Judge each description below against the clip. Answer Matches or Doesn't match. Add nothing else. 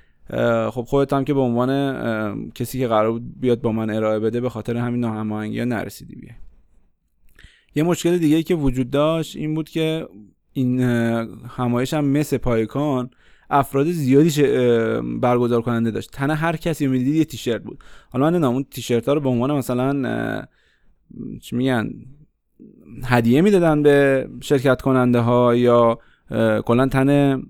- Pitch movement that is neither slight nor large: Matches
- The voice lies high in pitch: Doesn't match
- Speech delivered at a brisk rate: Doesn't match